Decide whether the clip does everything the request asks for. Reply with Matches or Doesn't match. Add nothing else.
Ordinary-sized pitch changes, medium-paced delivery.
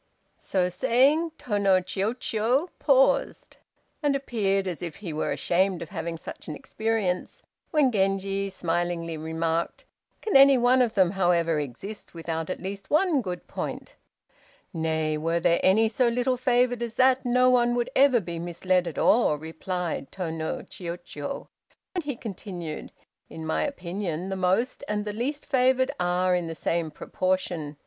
Doesn't match